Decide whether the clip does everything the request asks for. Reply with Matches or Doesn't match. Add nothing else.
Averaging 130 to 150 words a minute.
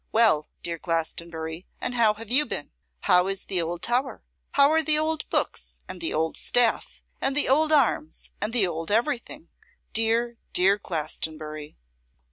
Doesn't match